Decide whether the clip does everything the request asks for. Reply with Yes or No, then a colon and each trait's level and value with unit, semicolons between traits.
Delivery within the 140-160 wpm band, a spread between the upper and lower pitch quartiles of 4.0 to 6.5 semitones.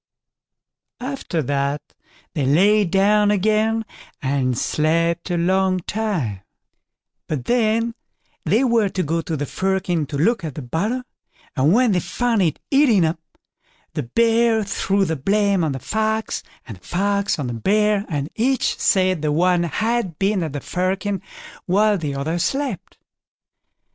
Yes: average, 150 wpm; wide, 5.5 semitones